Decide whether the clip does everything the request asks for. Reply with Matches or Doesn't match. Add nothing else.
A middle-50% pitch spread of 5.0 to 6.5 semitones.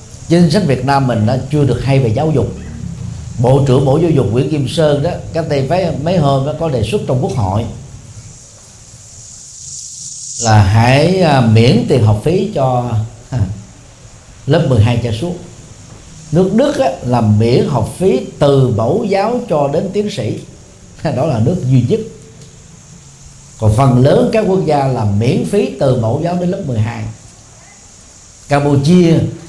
Matches